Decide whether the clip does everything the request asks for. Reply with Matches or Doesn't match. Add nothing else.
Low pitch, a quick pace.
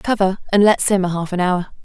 Doesn't match